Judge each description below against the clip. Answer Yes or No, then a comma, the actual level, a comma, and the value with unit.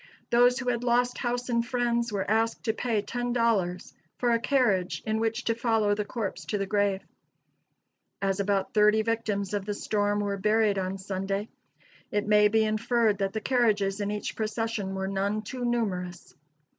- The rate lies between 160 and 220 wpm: Yes, average, 180 wpm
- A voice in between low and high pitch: No, high, 215 Hz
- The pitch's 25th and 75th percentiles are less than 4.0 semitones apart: Yes, average, 2.7 semitones